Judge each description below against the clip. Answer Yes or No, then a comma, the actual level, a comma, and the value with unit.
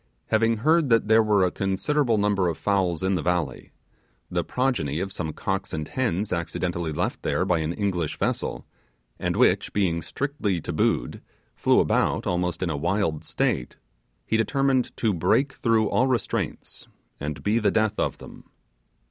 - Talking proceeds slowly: No, average, 165 wpm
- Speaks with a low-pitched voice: Yes, very low, 95 Hz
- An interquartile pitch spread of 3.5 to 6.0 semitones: Yes, average, 4.8 semitones